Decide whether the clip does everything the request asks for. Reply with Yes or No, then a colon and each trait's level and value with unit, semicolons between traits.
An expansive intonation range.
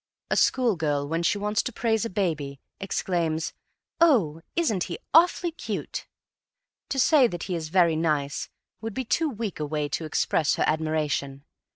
Yes: wide, 6.8 semitones